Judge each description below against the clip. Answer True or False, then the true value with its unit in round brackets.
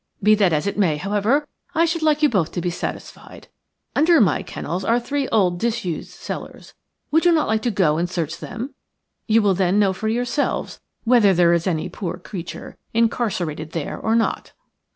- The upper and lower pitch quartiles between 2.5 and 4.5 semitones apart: False (5.4 semitones)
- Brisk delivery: False (190 wpm)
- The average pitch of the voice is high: True (205 Hz)